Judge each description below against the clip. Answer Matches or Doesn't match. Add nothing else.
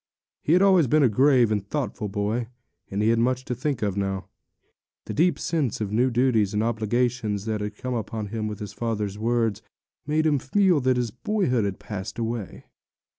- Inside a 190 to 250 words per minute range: Matches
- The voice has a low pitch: Matches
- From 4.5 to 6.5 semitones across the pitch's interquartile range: Doesn't match